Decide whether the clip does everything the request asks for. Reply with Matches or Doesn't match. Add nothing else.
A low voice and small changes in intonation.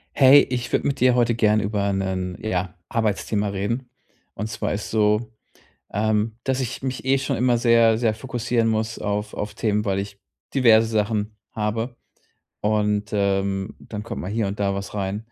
Matches